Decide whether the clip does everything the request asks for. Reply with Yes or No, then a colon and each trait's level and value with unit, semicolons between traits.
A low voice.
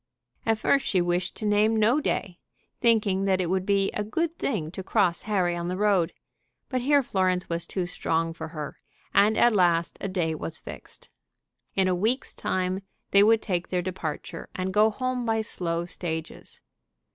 No: high, 190 Hz